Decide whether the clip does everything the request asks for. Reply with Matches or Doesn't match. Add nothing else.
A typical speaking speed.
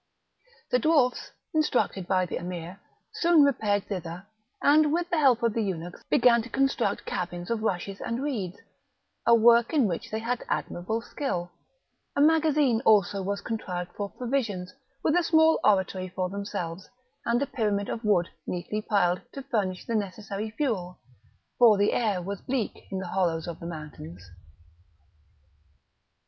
Matches